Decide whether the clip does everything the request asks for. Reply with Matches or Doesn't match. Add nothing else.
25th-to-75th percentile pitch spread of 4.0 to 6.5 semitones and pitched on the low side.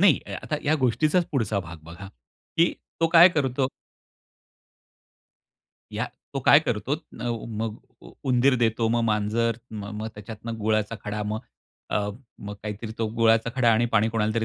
Doesn't match